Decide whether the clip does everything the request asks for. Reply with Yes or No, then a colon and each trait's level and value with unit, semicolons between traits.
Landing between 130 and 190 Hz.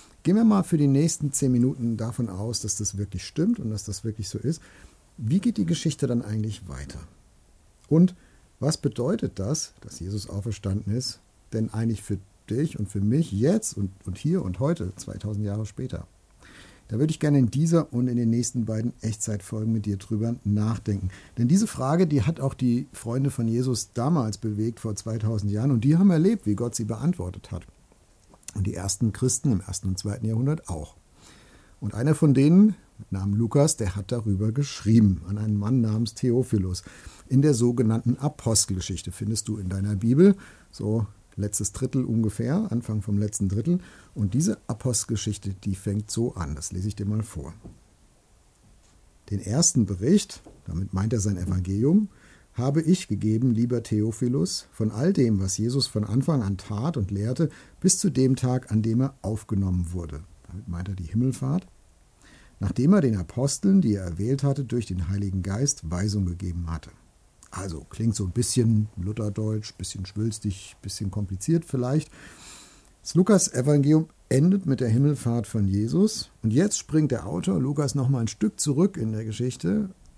No: low, 110 Hz